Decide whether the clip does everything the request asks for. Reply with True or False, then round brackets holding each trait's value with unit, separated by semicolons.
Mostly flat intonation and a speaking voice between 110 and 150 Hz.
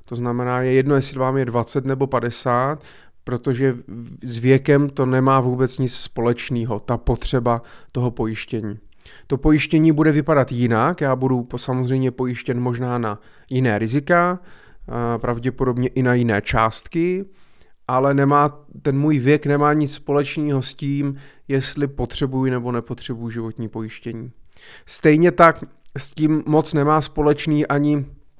False (3.2 semitones; 130 Hz)